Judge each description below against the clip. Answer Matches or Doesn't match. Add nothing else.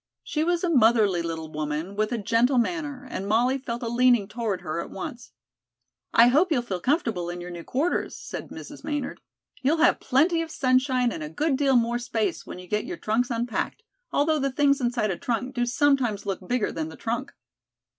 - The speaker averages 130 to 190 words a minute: Doesn't match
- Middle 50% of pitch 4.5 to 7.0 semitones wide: Matches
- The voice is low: Doesn't match